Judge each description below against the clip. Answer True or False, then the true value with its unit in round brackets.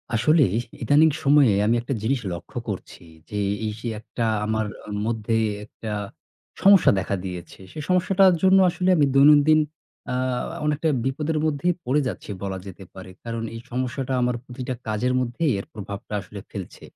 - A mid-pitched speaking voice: False (125 Hz)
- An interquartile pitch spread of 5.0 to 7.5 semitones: True (5.6 semitones)